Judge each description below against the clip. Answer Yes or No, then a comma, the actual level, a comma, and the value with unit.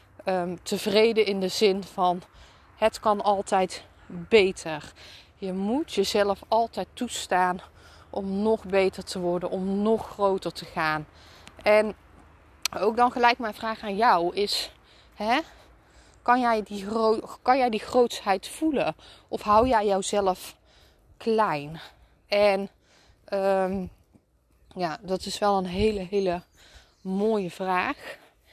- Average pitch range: Yes, average, 3.0 semitones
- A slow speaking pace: Yes, slow, 125 wpm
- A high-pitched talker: Yes, high, 195 Hz